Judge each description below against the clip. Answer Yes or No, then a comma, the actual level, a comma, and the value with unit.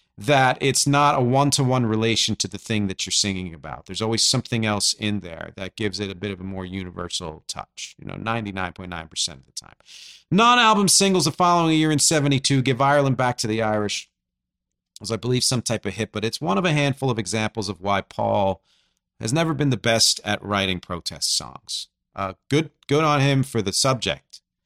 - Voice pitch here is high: No, low, 110 Hz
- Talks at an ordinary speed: No, fast, 210 wpm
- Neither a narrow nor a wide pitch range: No, wide, 6.1 semitones